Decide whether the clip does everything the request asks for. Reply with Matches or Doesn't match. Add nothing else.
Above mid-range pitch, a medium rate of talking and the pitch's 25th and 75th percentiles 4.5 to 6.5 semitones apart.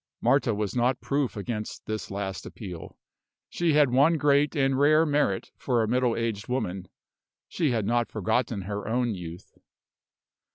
Doesn't match